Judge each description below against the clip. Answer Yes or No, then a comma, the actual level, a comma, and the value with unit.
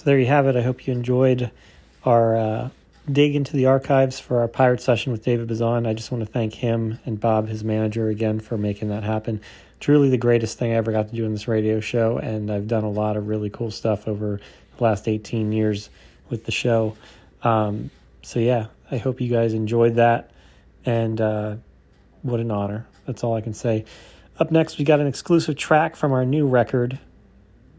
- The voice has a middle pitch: No, low, 115 Hz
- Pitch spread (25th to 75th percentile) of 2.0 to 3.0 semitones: Yes, narrow, 2.6 semitones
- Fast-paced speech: Yes, fast, 210 wpm